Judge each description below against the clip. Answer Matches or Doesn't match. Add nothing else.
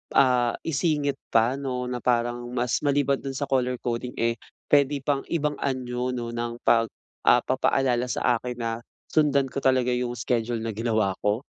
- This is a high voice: Doesn't match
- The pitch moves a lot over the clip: Doesn't match